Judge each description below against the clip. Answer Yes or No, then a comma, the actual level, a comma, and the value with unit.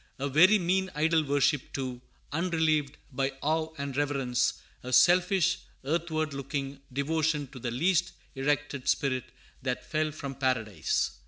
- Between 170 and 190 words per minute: No, slow, 135 wpm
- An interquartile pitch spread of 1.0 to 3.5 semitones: Yes, average, 3.0 semitones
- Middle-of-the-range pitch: Yes, medium, 145 Hz